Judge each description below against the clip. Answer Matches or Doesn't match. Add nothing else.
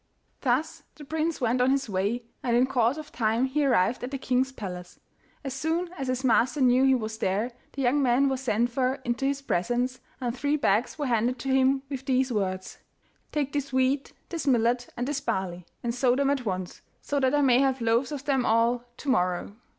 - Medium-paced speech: Doesn't match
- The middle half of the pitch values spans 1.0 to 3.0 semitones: Matches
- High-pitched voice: Matches